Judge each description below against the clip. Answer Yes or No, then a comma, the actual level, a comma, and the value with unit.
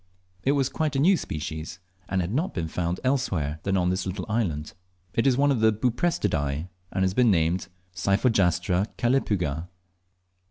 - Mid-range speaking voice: No, very low, 95 Hz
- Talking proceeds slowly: No, average, 165 wpm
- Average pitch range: No, wide, 6.5 semitones